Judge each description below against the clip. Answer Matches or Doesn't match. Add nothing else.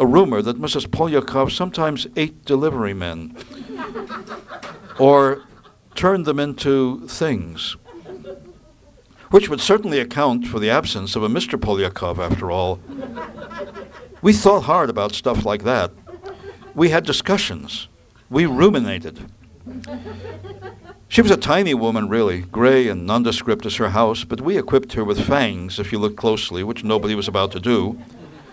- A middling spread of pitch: Doesn't match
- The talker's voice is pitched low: Matches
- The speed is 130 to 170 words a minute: Matches